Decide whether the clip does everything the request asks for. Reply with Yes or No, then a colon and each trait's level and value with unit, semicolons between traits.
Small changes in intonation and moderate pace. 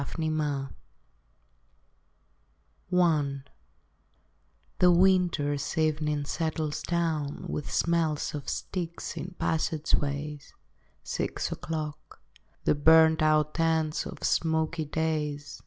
No: narrow, 1.6 semitones; slow, 85 wpm